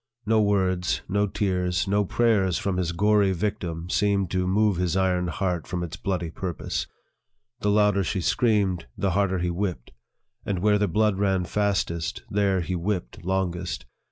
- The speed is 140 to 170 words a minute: Yes, average, 160 wpm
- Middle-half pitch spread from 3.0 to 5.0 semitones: No, narrow, 2.5 semitones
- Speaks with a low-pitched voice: Yes, very low, 95 Hz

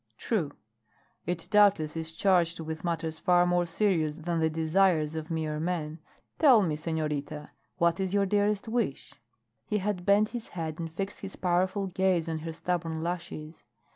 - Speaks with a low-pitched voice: No, medium, 170 Hz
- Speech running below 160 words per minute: No, average, 165 wpm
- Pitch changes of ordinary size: Yes, average, 3.2 semitones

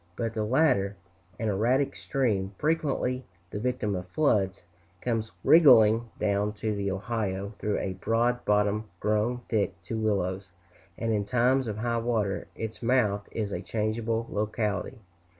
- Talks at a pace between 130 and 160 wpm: Yes, average, 145 wpm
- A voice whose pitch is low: Yes, low, 110 Hz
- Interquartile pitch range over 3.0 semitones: No, average, 2.7 semitones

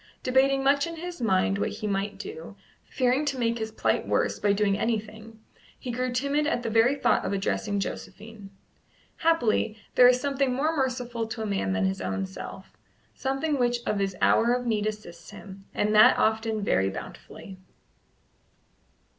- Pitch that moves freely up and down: No, average, 4.4 semitones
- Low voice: No, high, 225 Hz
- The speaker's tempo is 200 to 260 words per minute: No, average, 170 wpm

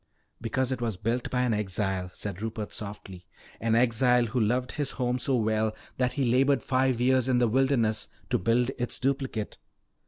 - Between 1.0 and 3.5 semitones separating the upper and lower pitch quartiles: Yes, average, 2.9 semitones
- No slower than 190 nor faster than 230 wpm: No, average, 180 wpm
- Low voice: Yes, low, 120 Hz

